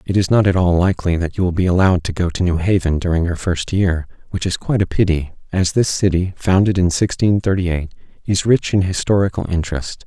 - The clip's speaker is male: Yes, male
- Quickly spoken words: Yes, fast, 225 wpm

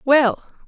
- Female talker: Yes, female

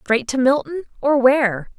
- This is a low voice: No, very high, 260 Hz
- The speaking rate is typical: Yes, average, 170 wpm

